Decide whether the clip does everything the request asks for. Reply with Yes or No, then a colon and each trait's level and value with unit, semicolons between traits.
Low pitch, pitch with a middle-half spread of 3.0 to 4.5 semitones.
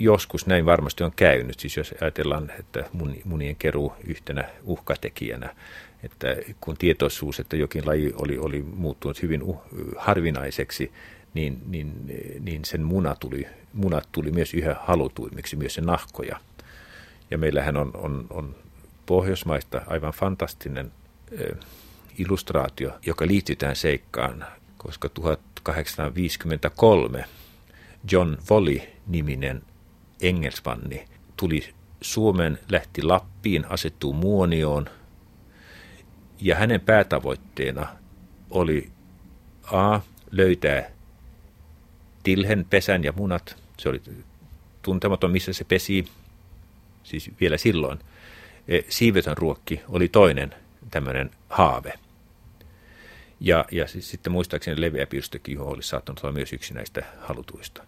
Yes: very low, 80 Hz; average, 4.0 semitones